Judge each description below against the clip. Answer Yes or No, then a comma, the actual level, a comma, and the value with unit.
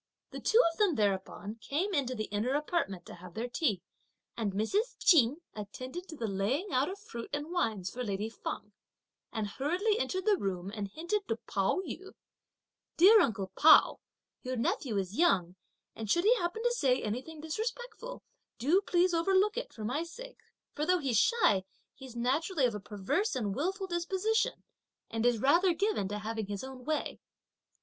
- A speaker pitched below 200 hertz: No, very high, 275 Hz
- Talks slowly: No, average, 175 wpm